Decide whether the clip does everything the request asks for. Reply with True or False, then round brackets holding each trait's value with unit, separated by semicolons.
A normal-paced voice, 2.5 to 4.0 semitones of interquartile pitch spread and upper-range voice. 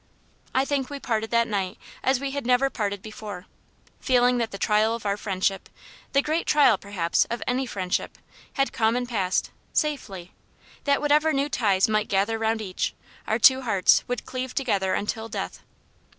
False (175 wpm; 4.6 semitones; 225 Hz)